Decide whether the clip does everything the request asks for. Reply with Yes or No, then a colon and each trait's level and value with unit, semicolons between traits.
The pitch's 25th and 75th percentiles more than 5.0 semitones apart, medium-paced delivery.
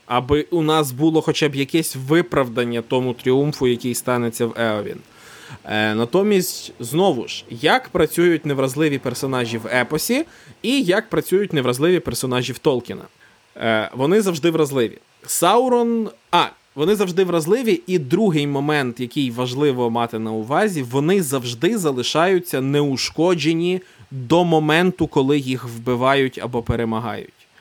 Yes: wide, 5.4 semitones; average, 130 wpm